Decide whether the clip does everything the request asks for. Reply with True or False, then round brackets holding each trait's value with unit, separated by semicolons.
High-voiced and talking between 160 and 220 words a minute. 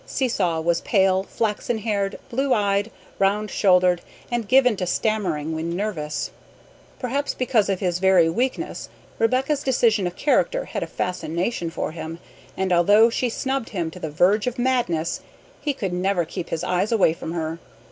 True (195 Hz; 165 wpm)